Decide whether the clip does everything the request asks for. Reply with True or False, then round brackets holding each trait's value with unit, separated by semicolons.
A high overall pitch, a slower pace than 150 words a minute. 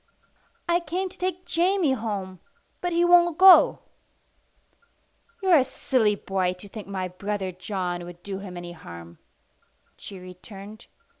True (205 Hz; 140 wpm)